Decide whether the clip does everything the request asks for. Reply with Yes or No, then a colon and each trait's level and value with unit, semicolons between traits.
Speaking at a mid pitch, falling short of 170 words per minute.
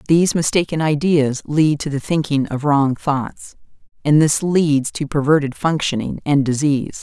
Yes: medium, 150 Hz; average, 155 wpm